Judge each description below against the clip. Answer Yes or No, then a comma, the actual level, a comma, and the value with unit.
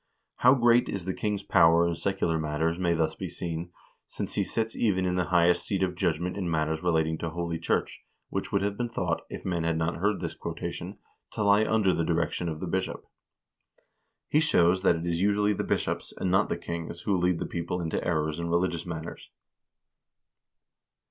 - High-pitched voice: No, very low, 85 Hz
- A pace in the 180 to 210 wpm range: Yes, average, 200 wpm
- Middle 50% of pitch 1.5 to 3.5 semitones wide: Yes, average, 2.7 semitones